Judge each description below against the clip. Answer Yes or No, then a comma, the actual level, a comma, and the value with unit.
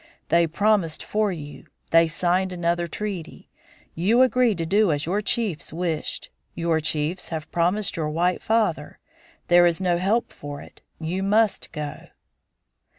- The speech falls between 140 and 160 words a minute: Yes, average, 150 wpm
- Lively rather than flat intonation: No, average, 4.0 semitones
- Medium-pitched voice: Yes, medium, 175 Hz